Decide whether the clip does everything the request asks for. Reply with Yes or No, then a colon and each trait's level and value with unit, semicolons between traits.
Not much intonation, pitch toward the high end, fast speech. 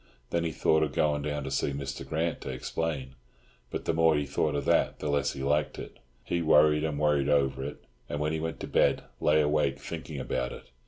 No: narrow, 1.8 semitones; very low, 75 Hz; fast, 225 wpm